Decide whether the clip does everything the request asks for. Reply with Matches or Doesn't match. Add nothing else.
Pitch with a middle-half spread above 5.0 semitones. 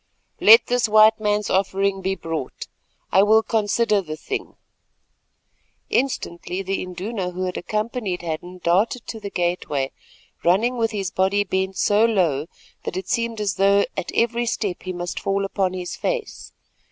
Doesn't match